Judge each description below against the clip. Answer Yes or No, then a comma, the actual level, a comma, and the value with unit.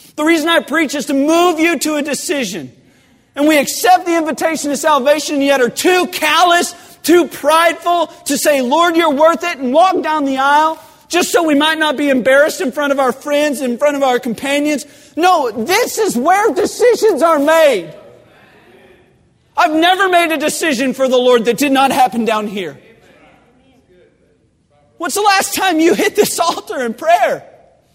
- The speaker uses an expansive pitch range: No, average, 3.6 semitones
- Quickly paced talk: No, average, 180 wpm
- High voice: Yes, very high, 310 Hz